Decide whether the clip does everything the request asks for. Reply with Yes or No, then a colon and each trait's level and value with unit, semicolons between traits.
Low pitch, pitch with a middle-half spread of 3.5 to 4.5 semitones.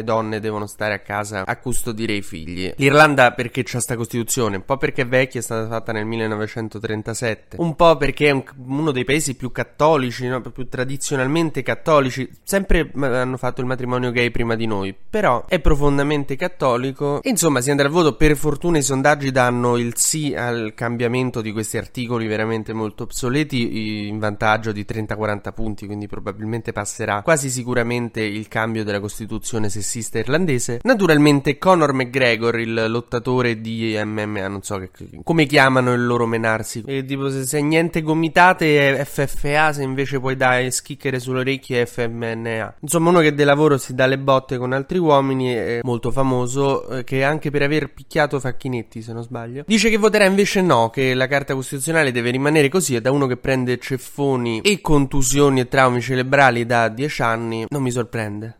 Yes: low, 125 Hz; average, 3.9 semitones